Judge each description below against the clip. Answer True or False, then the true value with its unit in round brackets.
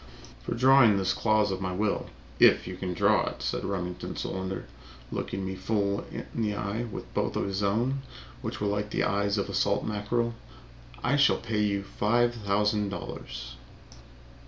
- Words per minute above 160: True (170 wpm)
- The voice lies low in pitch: True (100 Hz)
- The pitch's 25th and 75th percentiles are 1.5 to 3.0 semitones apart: True (2.4 semitones)